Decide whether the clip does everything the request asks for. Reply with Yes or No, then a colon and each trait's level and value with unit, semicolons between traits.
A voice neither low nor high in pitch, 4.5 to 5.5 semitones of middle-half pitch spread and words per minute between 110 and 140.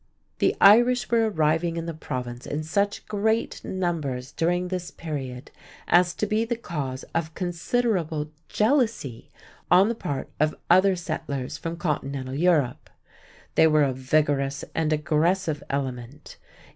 Yes: medium, 160 Hz; average, 5.0 semitones; slow, 135 wpm